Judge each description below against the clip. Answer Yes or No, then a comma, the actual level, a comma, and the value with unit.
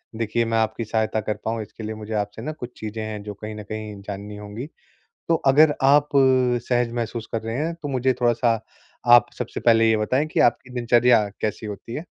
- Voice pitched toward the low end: Yes, low, 115 Hz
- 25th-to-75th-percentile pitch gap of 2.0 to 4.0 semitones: Yes, narrow, 2.5 semitones